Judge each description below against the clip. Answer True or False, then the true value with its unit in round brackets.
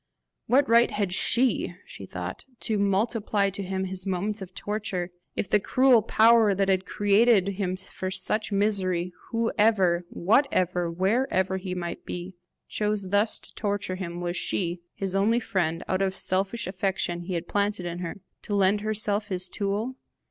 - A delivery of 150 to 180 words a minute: True (165 wpm)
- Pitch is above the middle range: True (195 Hz)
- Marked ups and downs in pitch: False (2.5 semitones)